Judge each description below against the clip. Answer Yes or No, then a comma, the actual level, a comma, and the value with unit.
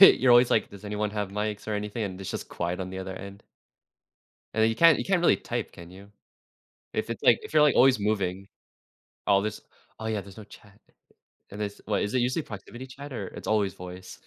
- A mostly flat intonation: No, average, 3.2 semitones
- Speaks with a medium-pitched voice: No, low, 105 Hz